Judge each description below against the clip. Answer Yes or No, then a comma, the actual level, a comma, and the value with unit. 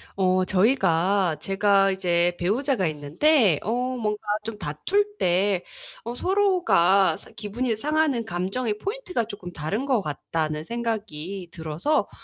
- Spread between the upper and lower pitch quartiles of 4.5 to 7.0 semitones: Yes, wide, 5.5 semitones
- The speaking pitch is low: No, high, 200 Hz